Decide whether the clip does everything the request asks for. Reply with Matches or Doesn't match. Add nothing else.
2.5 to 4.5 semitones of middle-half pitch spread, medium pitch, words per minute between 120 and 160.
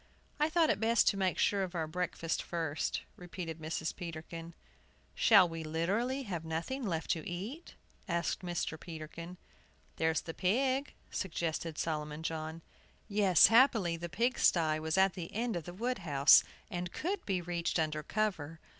Matches